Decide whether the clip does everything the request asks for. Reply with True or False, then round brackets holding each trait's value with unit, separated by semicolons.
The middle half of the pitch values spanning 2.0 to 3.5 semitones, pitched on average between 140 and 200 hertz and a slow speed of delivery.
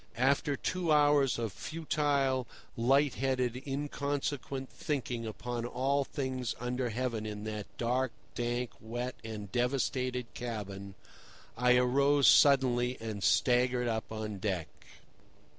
False (2.9 semitones; 125 Hz; 115 wpm)